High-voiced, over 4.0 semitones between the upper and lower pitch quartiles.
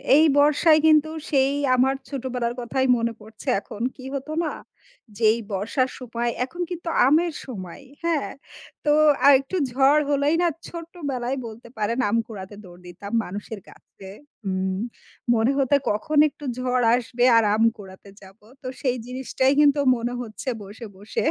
Yes: very high, 250 Hz; average, 4.6 semitones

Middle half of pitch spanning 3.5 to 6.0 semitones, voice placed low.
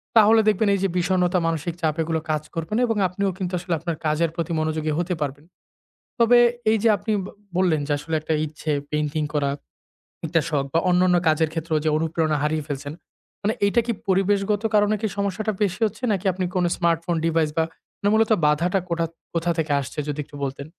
No: average, 3.9 semitones; medium, 170 Hz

